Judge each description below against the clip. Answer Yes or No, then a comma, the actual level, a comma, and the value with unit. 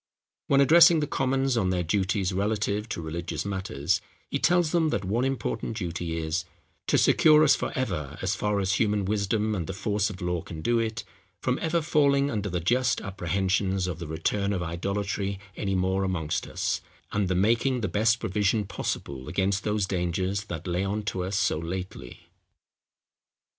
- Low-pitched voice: Yes, low, 100 Hz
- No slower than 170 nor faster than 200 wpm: Yes, average, 175 wpm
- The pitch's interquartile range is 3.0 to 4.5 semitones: Yes, average, 3.8 semitones